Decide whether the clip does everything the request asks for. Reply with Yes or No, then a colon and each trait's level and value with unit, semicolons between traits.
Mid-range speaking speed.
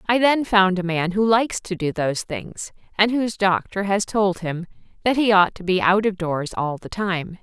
No: fast, 225 wpm